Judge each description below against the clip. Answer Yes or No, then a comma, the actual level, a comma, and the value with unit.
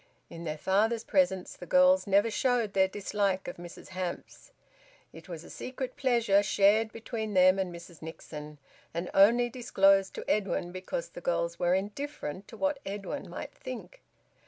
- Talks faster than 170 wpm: No, average, 160 wpm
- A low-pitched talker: No, high, 195 Hz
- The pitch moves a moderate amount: Yes, average, 4.5 semitones